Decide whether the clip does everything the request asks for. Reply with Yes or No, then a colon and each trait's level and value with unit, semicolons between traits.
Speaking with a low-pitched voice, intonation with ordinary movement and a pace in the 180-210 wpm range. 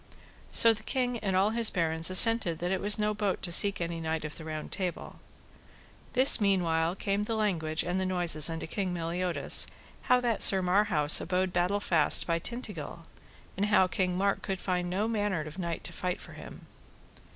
No: medium, 185 Hz; average, 3.6 semitones; average, 190 wpm